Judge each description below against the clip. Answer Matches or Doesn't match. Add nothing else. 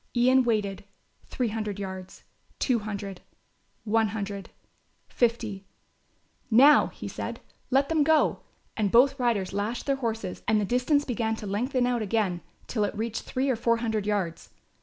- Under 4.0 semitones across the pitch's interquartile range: Matches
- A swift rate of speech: Doesn't match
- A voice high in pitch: Matches